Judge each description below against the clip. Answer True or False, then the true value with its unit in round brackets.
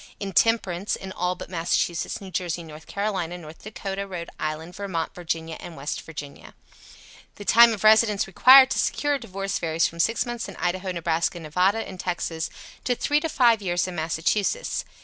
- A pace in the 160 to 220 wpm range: True (175 wpm)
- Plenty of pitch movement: False (4.2 semitones)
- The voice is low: False (185 Hz)